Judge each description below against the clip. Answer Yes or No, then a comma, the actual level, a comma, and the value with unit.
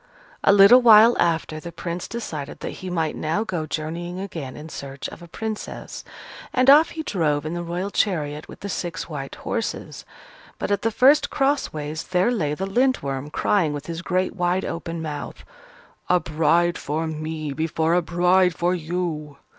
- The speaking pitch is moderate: Yes, medium, 170 Hz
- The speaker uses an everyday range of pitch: Yes, average, 4.0 semitones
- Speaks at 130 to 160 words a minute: No, average, 180 wpm